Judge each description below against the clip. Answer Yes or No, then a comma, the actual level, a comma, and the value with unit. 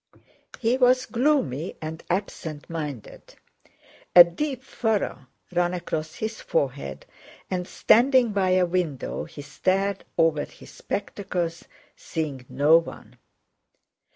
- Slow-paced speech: Yes, slow, 110 wpm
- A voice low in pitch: No, medium, 175 Hz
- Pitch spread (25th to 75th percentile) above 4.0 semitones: Yes, wide, 5.5 semitones